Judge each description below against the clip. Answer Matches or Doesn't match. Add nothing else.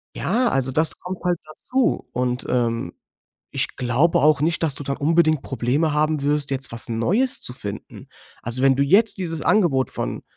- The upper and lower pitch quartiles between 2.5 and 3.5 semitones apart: Doesn't match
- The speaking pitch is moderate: Matches